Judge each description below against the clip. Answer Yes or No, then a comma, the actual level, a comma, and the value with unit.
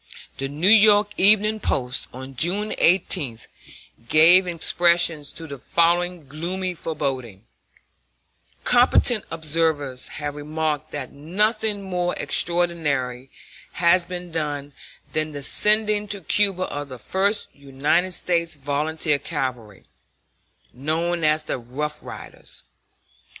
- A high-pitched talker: No, medium, 160 Hz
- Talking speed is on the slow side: Yes, slow, 110 wpm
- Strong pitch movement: No, average, 4.2 semitones